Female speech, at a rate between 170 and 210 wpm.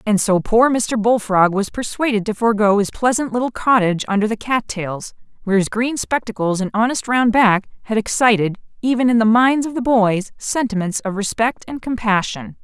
Yes: female; average, 185 wpm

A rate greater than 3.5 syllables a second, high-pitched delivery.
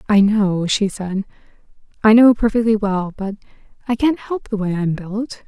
Yes: 4.6 syllables/s; high, 210 Hz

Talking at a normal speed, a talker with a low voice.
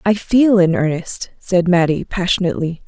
No: average, 145 wpm; medium, 185 Hz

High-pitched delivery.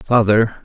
No: low, 110 Hz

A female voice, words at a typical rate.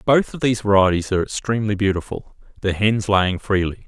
No: male; average, 170 wpm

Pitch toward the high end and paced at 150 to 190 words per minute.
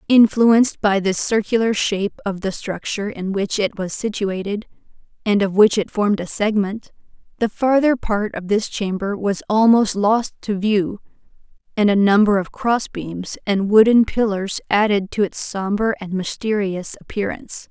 Yes: high, 205 Hz; average, 160 wpm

